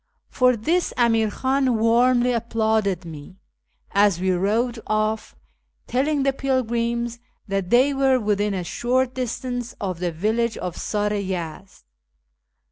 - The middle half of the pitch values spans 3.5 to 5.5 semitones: Yes, average, 3.9 semitones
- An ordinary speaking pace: No, slow, 130 wpm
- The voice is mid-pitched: No, high, 225 Hz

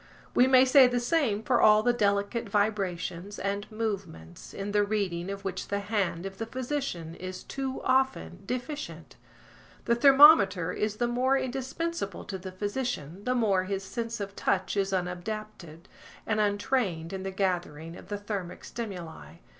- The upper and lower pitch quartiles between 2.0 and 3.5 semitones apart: No, average, 4.5 semitones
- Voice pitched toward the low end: No, high, 205 Hz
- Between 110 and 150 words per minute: No, average, 160 wpm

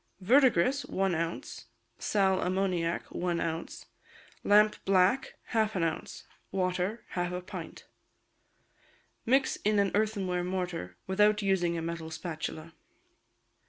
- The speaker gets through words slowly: Yes, slow, 110 wpm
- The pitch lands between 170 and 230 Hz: Yes, medium, 185 Hz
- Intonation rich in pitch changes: No, average, 3.4 semitones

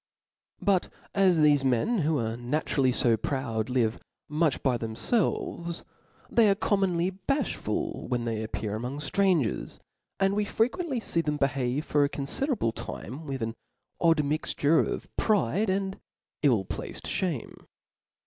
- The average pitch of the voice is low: No, medium, 150 Hz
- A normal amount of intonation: No, wide, 7.6 semitones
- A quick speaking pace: No, average, 140 wpm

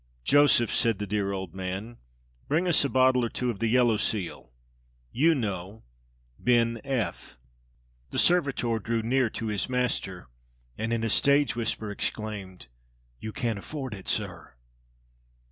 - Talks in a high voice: No, low, 115 Hz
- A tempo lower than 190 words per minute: Yes, average, 145 wpm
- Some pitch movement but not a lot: Yes, average, 3.8 semitones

